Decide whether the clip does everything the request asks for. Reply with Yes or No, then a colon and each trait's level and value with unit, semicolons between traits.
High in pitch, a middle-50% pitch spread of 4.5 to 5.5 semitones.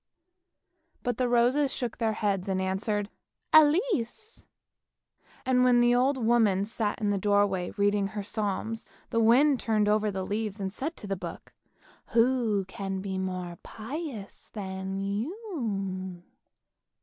No: high, 215 Hz; average, 4.0 semitones